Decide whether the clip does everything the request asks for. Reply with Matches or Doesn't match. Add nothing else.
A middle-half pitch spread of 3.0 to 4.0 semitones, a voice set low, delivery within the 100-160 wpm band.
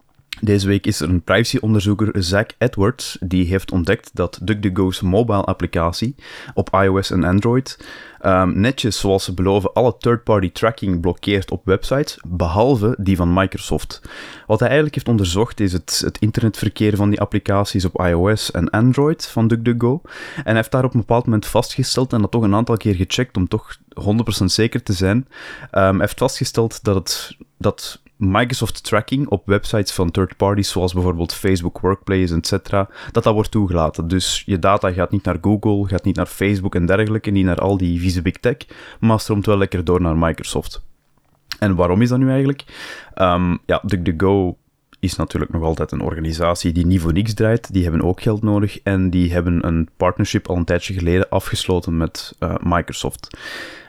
Doesn't match